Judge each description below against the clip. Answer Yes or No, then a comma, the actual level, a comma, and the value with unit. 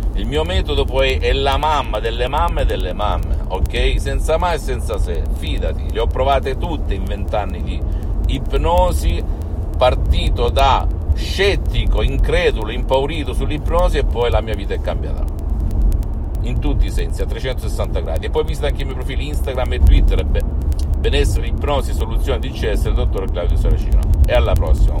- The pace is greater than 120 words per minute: Yes, average, 165 wpm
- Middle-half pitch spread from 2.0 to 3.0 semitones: Yes, narrow, 2.6 semitones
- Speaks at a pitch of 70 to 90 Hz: Yes, very low, 80 Hz